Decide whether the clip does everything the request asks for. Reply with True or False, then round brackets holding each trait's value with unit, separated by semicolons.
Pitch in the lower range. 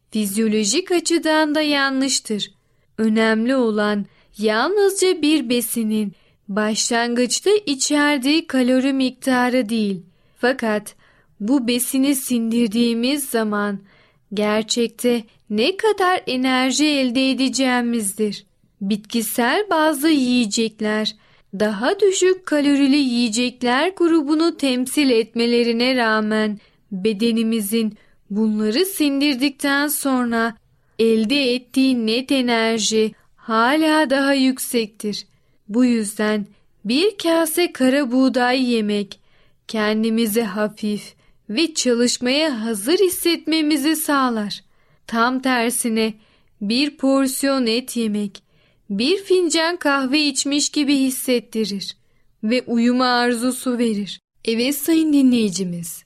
False (245 Hz)